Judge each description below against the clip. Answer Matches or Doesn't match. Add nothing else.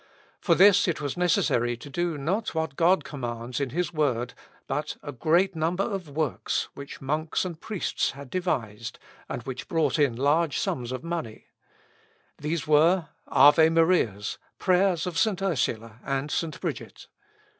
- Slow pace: Doesn't match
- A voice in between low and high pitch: Matches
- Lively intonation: Doesn't match